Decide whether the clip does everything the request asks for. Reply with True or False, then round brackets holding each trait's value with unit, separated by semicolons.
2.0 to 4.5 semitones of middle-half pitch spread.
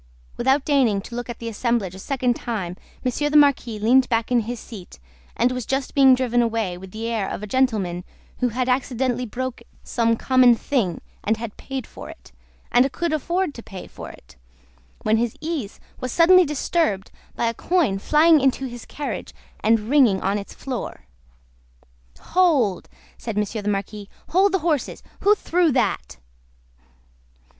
True (4.2 semitones)